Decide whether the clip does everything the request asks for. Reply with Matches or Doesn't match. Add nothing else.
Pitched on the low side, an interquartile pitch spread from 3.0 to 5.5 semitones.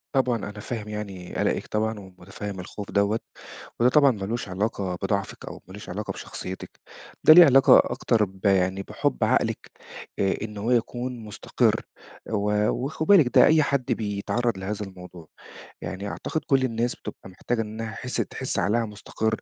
Matches